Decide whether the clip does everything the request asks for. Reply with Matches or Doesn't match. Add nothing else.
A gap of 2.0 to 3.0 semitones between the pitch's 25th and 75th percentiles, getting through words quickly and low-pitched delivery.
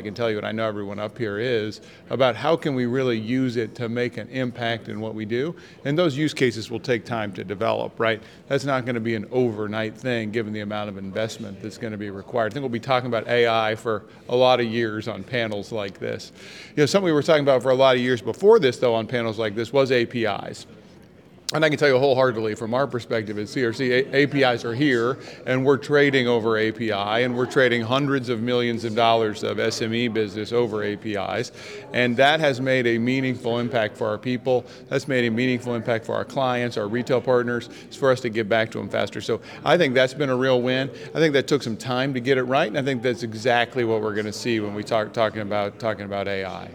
Matches